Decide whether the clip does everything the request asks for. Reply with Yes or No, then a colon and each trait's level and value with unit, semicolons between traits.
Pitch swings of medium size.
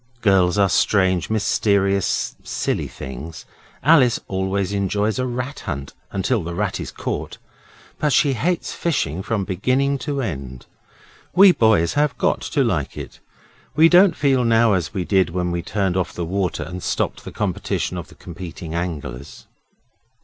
No: wide, 6.4 semitones